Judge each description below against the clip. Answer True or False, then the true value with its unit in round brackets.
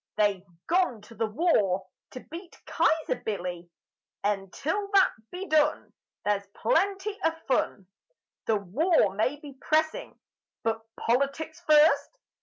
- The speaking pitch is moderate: False (280 Hz)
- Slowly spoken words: True (125 wpm)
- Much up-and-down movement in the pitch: True (7.9 semitones)